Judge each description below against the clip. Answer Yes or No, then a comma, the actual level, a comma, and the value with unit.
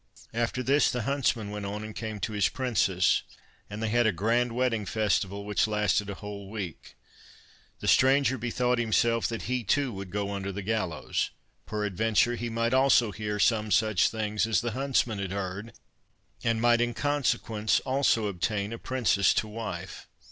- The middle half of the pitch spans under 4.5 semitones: Yes, average, 2.8 semitones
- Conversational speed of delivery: Yes, average, 170 wpm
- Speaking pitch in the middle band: No, low, 110 Hz